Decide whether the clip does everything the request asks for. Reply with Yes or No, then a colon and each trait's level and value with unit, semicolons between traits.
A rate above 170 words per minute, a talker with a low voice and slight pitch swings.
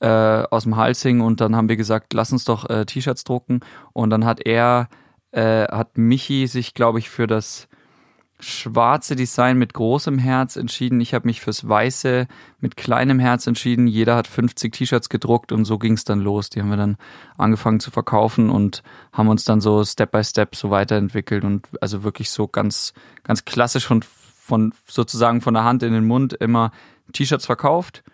Yes: fast, 190 wpm; low, 115 Hz; narrow, 2.2 semitones